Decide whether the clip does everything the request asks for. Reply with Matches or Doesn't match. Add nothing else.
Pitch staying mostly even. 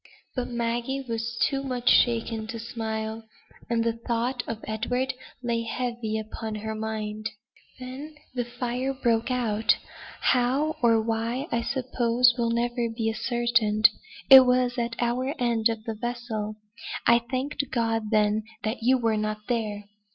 Matches